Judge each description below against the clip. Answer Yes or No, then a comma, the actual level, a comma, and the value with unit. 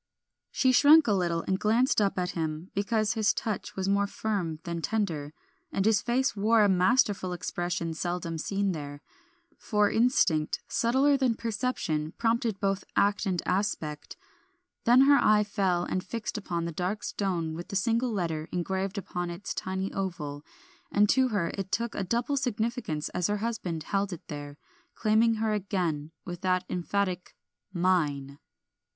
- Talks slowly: No, average, 160 wpm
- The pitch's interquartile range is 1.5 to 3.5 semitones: No, average, 4.3 semitones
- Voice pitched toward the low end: No, high, 195 Hz